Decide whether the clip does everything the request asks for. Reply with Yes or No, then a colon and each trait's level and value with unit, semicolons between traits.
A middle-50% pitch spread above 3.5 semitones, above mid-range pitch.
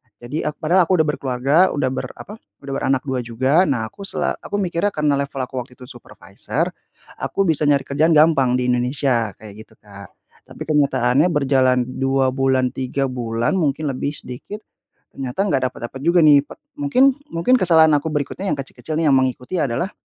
No: average, 4.0 semitones; medium, 140 Hz